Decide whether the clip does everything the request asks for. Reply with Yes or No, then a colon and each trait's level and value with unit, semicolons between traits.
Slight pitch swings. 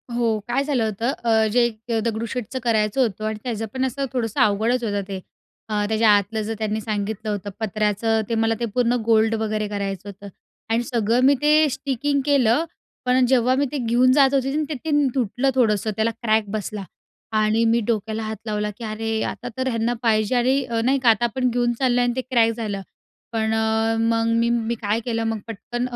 Yes: narrow, 2.3 semitones